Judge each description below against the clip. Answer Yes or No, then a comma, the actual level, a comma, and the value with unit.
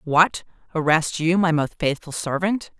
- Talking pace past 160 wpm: No, average, 150 wpm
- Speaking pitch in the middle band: Yes, medium, 165 Hz